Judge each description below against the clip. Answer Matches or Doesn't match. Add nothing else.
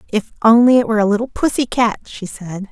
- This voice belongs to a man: Doesn't match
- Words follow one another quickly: Matches